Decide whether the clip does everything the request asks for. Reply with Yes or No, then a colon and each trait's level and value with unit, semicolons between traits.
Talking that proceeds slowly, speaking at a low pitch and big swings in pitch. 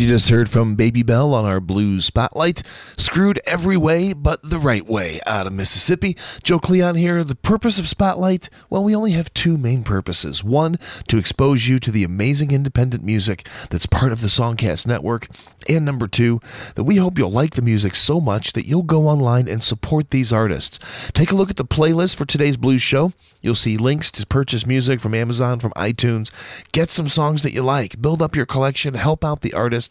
No: fast, 205 wpm; low, 130 Hz; wide, 5.8 semitones